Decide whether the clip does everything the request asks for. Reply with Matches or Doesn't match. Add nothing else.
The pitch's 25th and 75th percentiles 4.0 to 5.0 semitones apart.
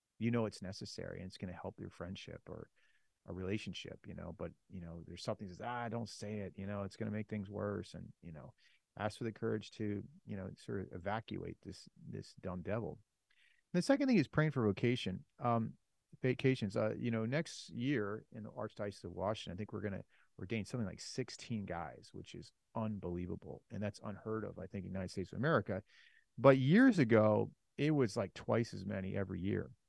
Doesn't match